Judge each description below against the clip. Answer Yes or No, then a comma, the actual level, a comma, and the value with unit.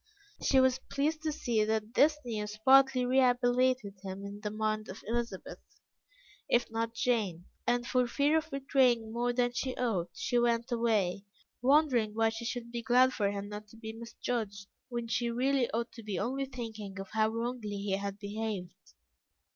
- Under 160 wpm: No, average, 180 wpm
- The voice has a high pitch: Yes, high, 235 Hz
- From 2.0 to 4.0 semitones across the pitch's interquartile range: Yes, average, 3.0 semitones